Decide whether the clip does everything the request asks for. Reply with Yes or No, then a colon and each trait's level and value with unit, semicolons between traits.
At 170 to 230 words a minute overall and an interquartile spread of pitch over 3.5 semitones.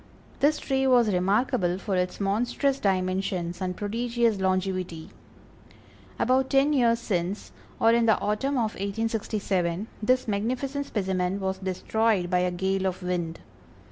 No: slow, 135 wpm; average, 4.2 semitones